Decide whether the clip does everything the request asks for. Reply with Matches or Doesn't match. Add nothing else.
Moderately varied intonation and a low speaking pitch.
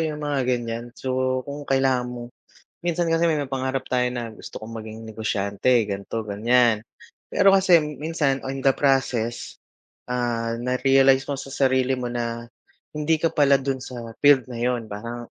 Matches